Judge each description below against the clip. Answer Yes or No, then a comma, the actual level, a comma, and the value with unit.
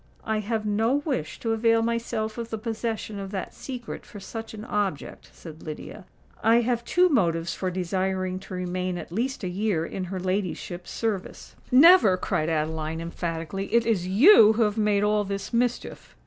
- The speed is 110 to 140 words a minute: No, average, 175 wpm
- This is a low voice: No, high, 205 Hz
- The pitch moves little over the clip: No, average, 3.8 semitones